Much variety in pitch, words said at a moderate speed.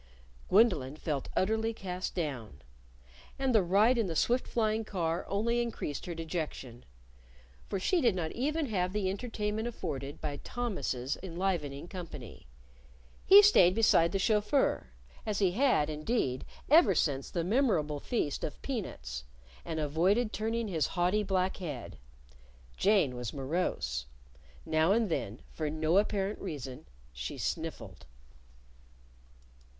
No: wide, 6.4 semitones; slow, 130 wpm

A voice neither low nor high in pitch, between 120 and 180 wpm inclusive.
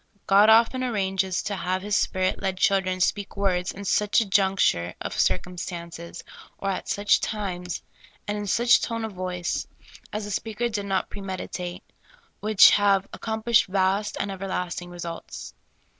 No: high, 195 Hz; average, 175 wpm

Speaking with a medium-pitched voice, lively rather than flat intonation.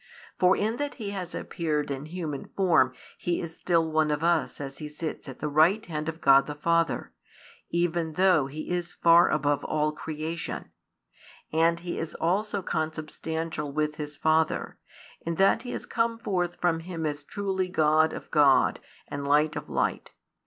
No: medium, 160 Hz; narrow, 2.6 semitones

